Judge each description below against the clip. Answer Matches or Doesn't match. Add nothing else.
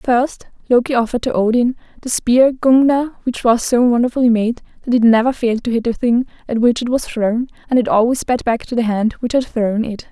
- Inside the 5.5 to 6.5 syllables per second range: Matches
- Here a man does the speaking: Doesn't match